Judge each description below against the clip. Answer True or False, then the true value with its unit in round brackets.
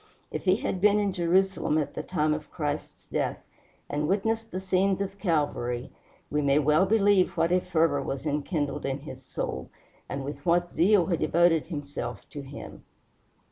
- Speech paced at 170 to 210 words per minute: True (175 wpm)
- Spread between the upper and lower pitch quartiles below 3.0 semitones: False (4.6 semitones)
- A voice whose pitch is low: False (165 Hz)